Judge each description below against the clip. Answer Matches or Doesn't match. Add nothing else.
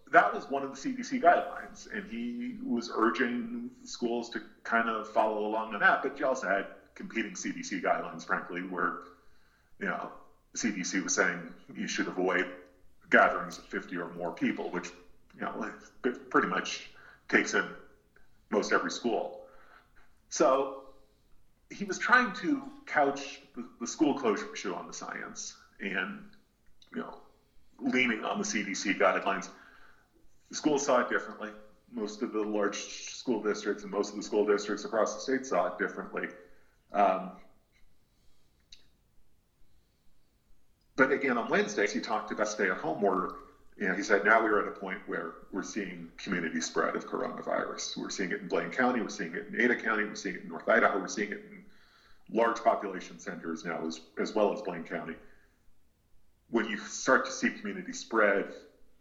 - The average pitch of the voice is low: Matches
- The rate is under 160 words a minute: Doesn't match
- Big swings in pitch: Matches